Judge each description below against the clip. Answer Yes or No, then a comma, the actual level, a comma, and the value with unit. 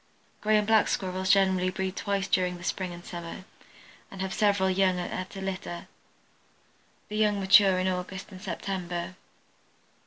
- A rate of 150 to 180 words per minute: Yes, average, 155 wpm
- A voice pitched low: No, high, 190 Hz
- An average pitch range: No, narrow, 1.2 semitones